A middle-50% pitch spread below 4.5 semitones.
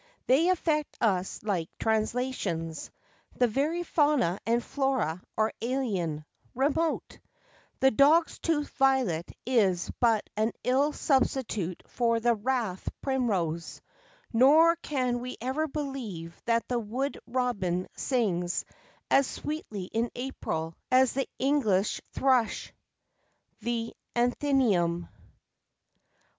No: average, 5.3 semitones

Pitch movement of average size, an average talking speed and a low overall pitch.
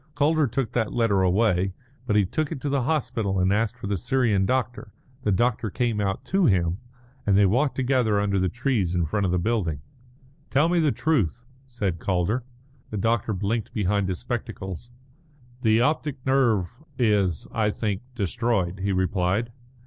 Yes: average, 4.4 semitones; average, 170 wpm; low, 110 Hz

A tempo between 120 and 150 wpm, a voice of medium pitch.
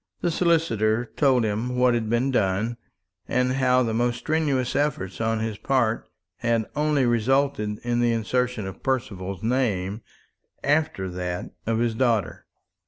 No: average, 145 wpm; low, 120 Hz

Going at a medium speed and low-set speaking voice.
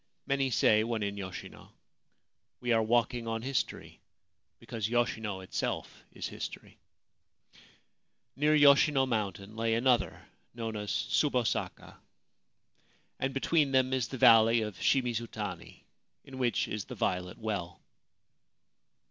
No: slow, 120 wpm; low, 115 Hz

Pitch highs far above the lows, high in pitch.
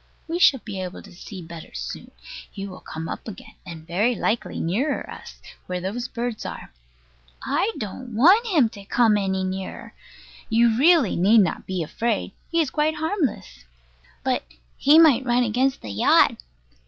Yes: wide, 6.1 semitones; high, 225 Hz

